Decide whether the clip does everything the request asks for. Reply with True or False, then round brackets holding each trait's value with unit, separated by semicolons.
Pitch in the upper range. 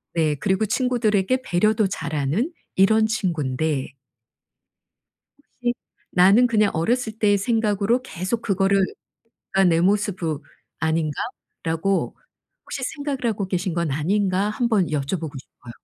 True (195 Hz)